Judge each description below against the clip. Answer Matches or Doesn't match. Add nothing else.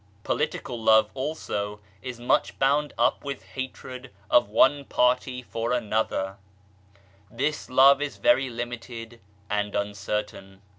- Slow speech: Matches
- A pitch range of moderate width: Matches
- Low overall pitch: Matches